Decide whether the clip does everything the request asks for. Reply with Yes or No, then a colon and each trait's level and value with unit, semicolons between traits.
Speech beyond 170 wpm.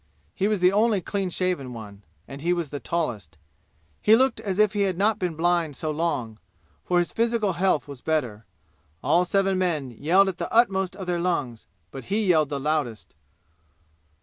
Yes: average, 185 wpm